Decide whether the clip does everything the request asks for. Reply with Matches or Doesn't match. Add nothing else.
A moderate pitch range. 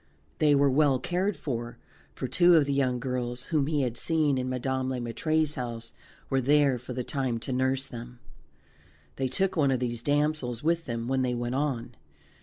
Matches